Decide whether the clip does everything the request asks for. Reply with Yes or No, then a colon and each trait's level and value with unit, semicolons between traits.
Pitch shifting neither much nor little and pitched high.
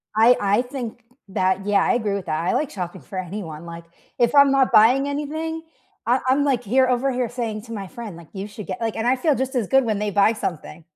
Yes: average, 4.8 semitones; high, 230 Hz